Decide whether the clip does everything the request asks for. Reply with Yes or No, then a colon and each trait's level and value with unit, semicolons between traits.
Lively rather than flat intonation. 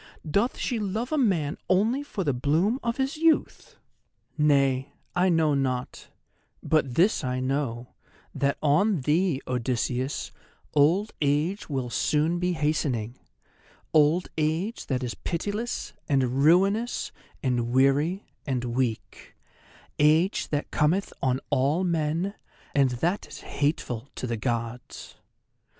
Yes: wide, 5.9 semitones